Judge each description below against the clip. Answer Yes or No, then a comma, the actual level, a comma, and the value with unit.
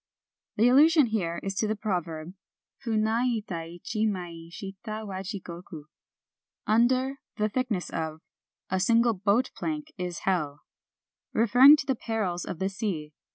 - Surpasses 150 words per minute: No, average, 145 wpm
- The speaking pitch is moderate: No, high, 205 Hz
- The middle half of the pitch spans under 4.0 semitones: No, average, 4.8 semitones